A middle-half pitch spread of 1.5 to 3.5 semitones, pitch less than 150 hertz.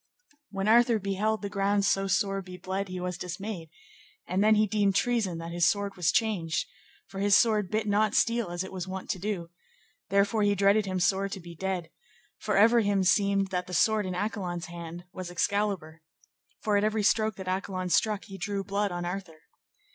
No: narrow, 2.4 semitones; high, 195 Hz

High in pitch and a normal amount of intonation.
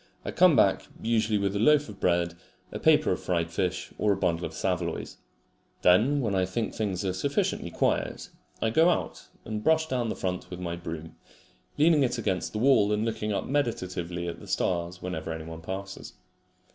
No: low, 100 Hz; average, 4.5 semitones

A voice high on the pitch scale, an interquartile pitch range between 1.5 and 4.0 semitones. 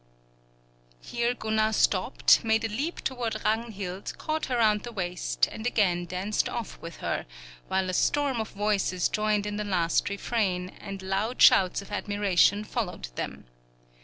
Yes: high, 210 Hz; average, 3.0 semitones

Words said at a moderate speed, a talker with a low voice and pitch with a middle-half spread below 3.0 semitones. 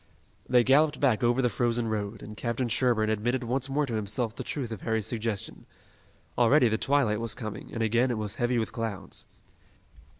Yes: average, 190 wpm; low, 115 Hz; narrow, 2.5 semitones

